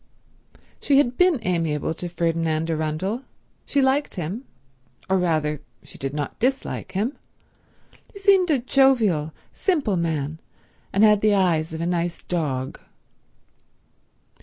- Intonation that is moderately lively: No, wide, 8.0 semitones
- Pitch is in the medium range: Yes, medium, 175 Hz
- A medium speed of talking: No, slow, 125 wpm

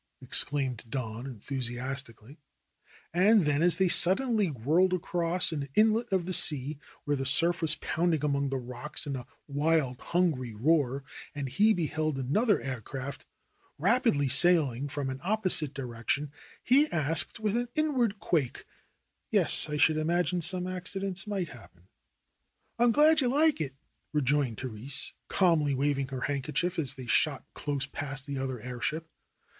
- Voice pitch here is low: No, medium, 150 Hz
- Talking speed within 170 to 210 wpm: No, average, 155 wpm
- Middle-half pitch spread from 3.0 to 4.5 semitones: No, average, 5.3 semitones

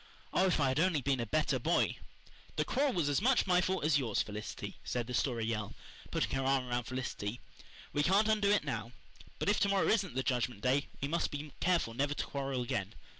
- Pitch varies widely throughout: Yes, wide, 6.6 semitones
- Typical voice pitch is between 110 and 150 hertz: Yes, medium, 140 Hz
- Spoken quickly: Yes, fast, 225 wpm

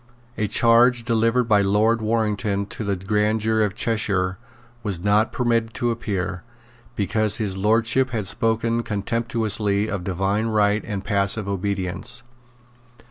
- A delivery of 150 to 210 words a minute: No, slow, 135 wpm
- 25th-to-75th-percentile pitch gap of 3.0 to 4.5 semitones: No, narrow, 2.4 semitones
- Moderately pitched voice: No, low, 110 Hz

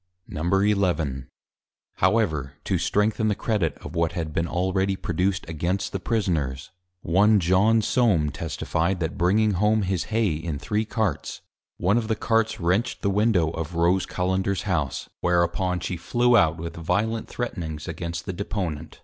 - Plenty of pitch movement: No, average, 4.0 semitones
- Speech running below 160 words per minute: Yes, average, 150 wpm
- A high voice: No, very low, 90 Hz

